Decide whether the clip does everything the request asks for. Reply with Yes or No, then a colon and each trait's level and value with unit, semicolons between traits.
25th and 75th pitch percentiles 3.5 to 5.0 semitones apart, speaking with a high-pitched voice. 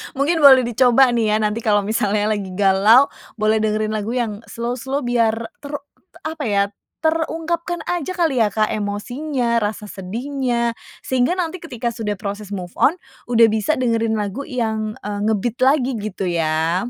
Yes: average, 4.2 semitones; high, 230 Hz